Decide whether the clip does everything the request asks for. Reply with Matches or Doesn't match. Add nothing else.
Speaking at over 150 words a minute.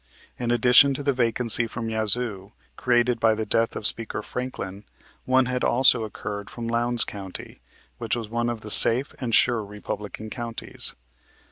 Matches